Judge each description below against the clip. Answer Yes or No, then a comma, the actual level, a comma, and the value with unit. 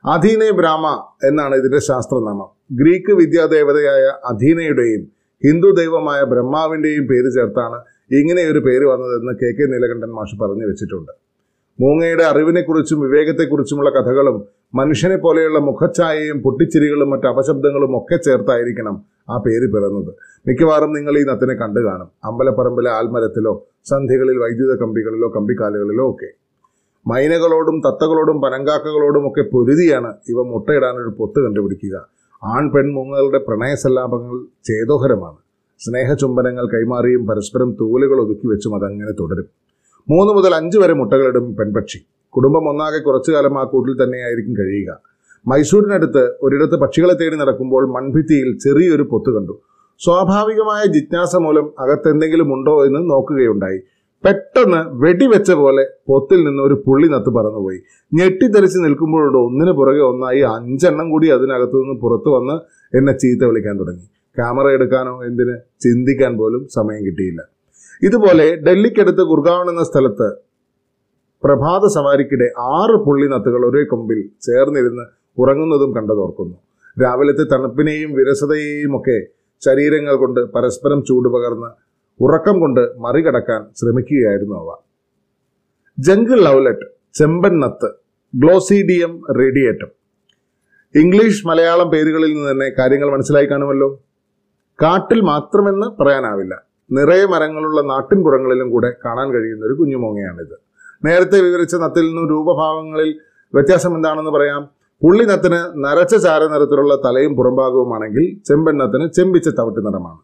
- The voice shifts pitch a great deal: No, average, 4.3 semitones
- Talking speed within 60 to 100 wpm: No, average, 110 wpm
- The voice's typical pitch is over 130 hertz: Yes, medium, 140 Hz